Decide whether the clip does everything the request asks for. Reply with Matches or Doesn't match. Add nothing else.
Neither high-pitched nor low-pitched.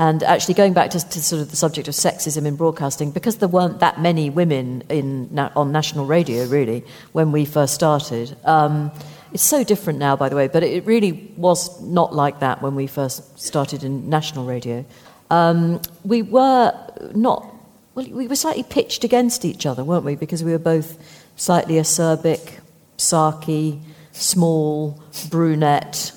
Matches